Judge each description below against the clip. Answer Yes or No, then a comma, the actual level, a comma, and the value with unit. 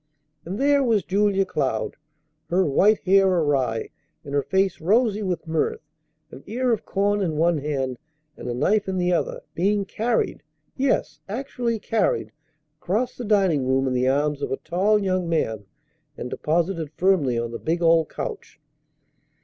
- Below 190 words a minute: Yes, average, 165 wpm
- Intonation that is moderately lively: No, wide, 6.0 semitones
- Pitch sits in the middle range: Yes, medium, 180 Hz